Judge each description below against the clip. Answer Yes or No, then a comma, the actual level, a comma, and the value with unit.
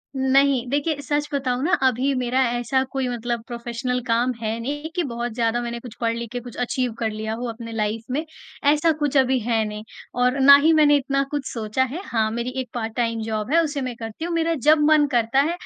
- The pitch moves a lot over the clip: No, average, 3.4 semitones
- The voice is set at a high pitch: Yes, very high, 250 Hz